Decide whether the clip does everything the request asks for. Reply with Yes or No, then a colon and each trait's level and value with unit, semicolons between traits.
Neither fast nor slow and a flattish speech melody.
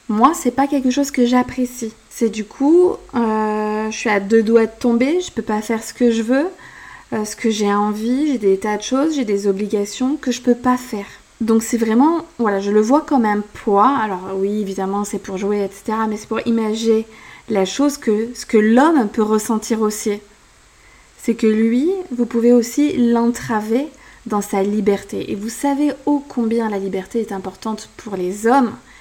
No: average, 200 wpm; average, 3.1 semitones